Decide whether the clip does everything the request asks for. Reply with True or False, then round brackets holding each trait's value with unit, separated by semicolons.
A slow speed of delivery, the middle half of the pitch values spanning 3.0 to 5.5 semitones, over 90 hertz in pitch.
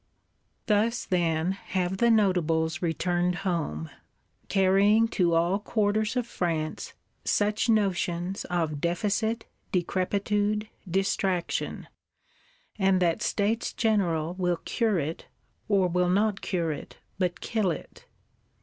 True (110 wpm; 3.3 semitones; 185 Hz)